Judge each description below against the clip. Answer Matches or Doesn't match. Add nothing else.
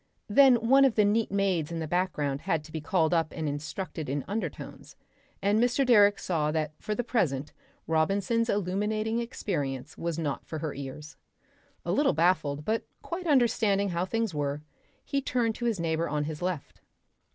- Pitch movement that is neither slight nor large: Doesn't match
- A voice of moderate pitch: Matches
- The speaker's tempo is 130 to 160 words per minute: Doesn't match